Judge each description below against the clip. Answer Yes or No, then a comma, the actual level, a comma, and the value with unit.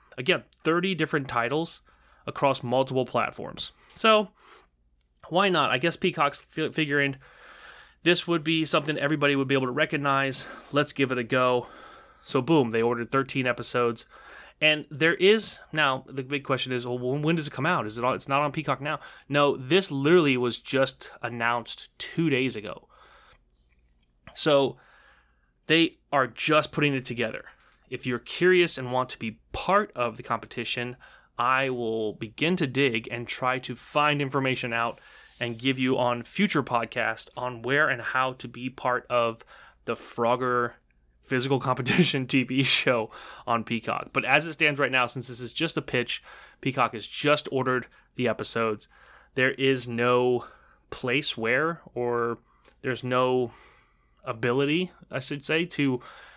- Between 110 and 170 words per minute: Yes, average, 160 wpm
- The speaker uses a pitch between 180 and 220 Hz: No, low, 130 Hz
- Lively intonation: No, average, 3.6 semitones